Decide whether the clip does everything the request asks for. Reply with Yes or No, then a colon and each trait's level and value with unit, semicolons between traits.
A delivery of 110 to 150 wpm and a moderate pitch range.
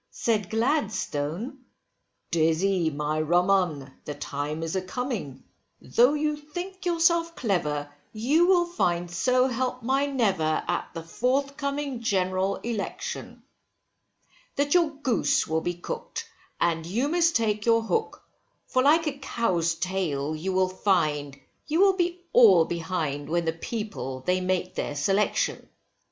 No: average, 140 wpm; wide, 9.0 semitones